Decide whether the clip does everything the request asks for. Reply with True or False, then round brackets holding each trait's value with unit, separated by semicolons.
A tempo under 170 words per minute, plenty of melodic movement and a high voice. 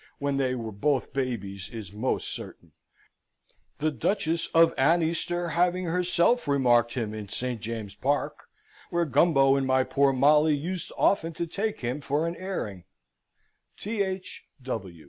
False (140 wpm; 5.8 semitones; 140 Hz)